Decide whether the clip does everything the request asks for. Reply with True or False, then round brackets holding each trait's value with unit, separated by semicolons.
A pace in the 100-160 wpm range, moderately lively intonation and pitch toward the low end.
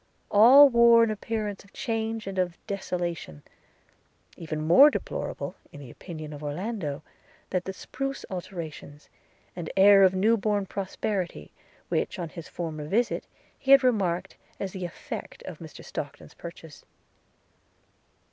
False (140 wpm; 4.9 semitones; 190 Hz)